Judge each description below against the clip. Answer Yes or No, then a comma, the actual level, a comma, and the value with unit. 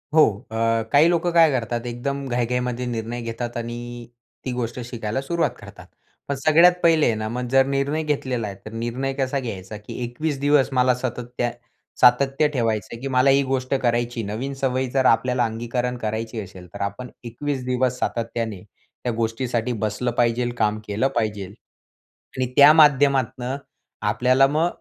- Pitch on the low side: Yes, low, 125 Hz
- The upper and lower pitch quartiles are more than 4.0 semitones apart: No, average, 2.9 semitones